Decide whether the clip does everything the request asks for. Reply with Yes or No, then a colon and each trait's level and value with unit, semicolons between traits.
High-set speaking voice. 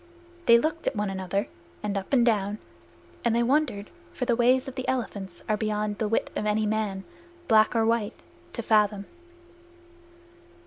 Yes: high, 215 Hz